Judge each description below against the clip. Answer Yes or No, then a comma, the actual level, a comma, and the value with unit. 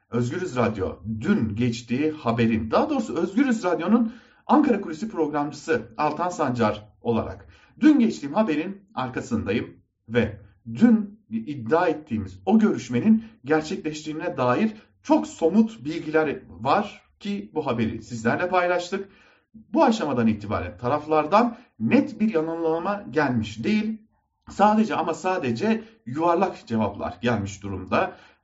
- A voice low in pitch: No, medium, 160 Hz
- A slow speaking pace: Yes, slow, 110 wpm